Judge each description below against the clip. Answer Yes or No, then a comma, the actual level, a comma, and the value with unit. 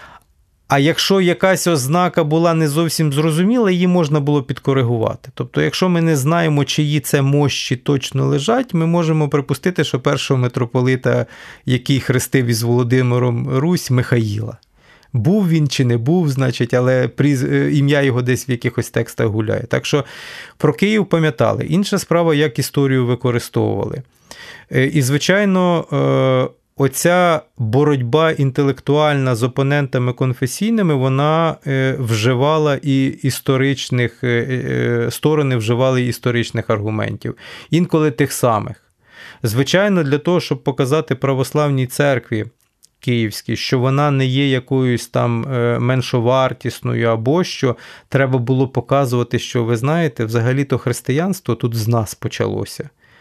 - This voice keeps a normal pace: Yes, average, 120 wpm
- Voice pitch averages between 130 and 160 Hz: Yes, low, 135 Hz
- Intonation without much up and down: No, average, 3.8 semitones